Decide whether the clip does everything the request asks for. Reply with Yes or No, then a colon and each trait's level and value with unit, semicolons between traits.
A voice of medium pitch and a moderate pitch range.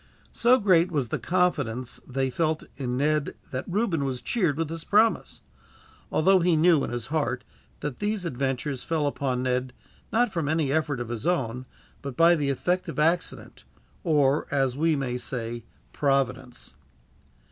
Yes: medium, 145 Hz; average, 4.6 semitones